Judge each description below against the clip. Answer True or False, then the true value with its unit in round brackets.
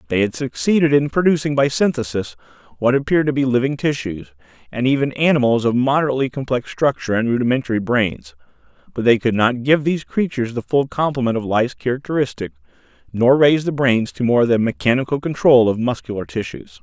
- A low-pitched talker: True (125 Hz)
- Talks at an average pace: True (170 wpm)